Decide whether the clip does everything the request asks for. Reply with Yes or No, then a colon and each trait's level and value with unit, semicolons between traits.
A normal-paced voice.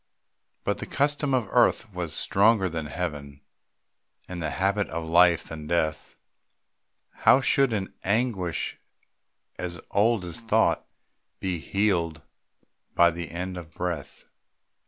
No: slow, 125 wpm